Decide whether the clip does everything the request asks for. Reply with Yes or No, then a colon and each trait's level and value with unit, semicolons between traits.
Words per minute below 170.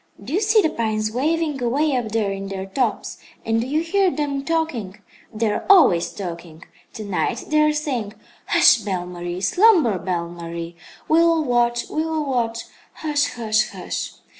No: average, 175 wpm